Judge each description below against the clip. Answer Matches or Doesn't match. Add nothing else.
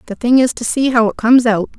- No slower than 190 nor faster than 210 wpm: Doesn't match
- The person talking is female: Matches